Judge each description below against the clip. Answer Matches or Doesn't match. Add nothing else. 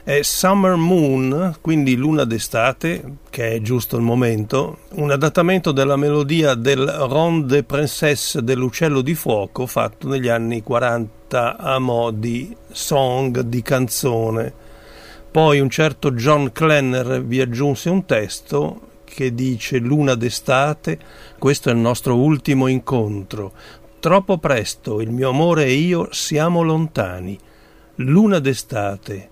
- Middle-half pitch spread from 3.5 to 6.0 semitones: Matches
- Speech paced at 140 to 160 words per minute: Doesn't match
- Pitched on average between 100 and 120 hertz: Doesn't match